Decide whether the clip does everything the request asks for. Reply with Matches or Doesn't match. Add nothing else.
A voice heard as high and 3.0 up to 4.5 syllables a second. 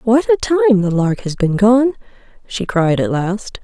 Matches